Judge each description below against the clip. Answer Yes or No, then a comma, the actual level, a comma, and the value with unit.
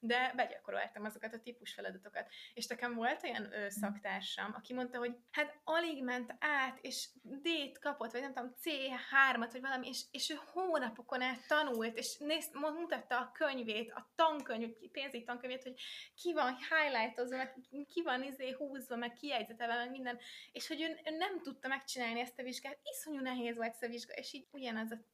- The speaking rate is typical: No, fast, 180 wpm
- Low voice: No, very high, 255 Hz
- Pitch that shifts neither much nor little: Yes, average, 3.3 semitones